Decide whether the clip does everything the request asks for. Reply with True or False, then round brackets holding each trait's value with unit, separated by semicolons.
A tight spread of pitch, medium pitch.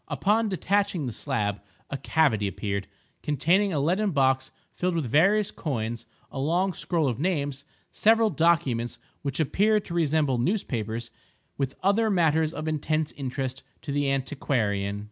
False (5.4 semitones; 150 Hz)